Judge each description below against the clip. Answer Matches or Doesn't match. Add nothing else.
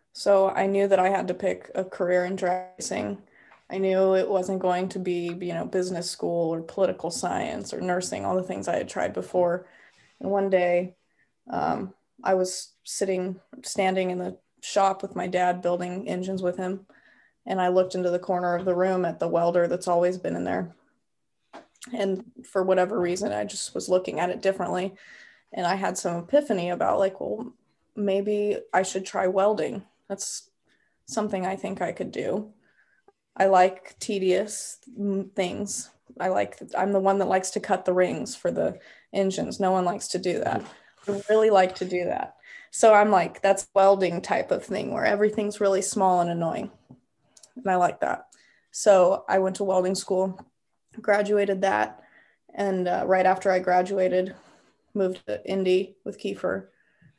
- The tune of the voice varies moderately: Doesn't match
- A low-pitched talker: Doesn't match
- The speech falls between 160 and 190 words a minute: Matches